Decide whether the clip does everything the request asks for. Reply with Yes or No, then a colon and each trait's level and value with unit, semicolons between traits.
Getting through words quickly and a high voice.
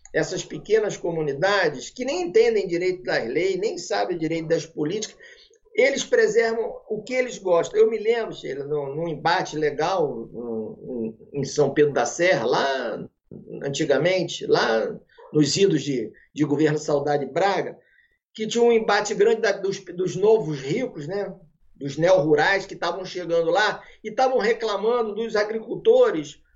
No: average, 155 wpm; high, 200 Hz